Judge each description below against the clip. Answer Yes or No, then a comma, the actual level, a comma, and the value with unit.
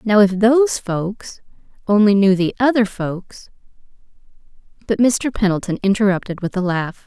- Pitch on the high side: Yes, high, 205 Hz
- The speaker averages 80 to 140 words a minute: Yes, slow, 135 wpm